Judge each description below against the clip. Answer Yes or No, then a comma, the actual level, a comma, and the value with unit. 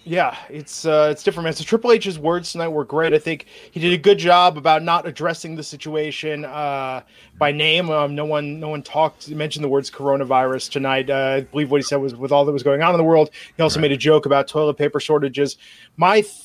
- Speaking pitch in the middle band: Yes, medium, 150 Hz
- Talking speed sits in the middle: No, fast, 240 wpm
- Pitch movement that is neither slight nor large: No, narrow, 2.3 semitones